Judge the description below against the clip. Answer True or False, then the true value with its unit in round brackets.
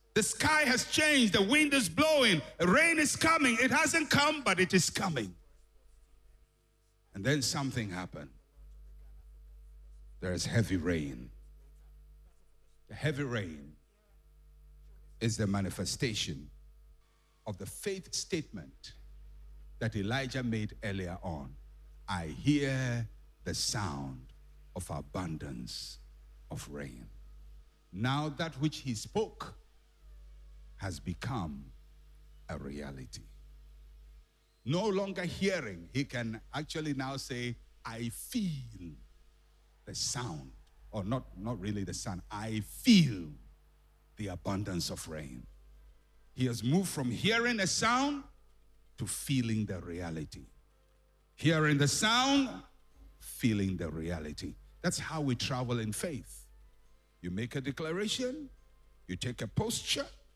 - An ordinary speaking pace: False (115 wpm)